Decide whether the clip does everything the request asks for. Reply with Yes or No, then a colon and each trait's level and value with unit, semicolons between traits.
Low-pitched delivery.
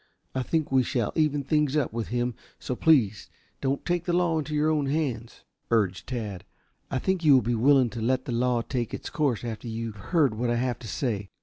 Yes: low, 125 Hz